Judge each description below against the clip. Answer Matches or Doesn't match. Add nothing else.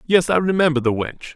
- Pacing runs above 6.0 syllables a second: Doesn't match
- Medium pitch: Matches